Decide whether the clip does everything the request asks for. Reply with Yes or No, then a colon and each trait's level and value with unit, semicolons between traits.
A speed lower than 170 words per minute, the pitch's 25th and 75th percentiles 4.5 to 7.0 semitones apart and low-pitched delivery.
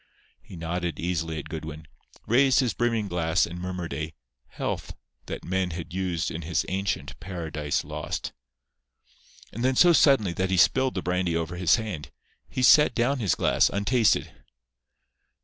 Yes: average, 155 wpm; average, 5.2 semitones; very low, 90 Hz